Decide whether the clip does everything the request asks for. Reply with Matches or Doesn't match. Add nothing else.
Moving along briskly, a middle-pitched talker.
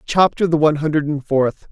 Matches